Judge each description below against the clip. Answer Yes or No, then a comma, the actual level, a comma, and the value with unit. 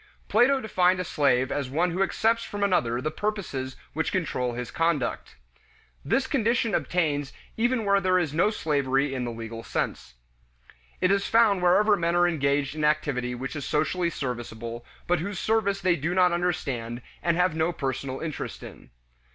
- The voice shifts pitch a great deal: Yes, wide, 6.0 semitones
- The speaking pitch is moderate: Yes, medium, 165 Hz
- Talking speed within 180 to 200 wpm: No, average, 170 wpm